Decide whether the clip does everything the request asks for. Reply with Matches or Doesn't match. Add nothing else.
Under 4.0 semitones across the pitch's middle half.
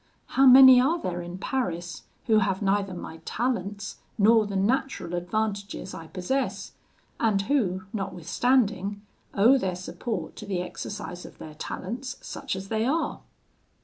Doesn't match